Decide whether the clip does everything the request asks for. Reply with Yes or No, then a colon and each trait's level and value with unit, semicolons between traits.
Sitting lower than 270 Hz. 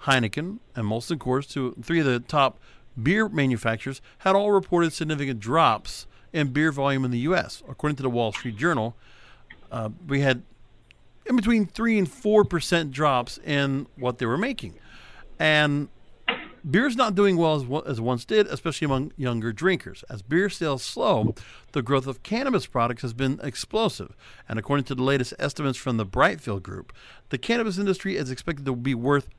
Yes: medium, 140 Hz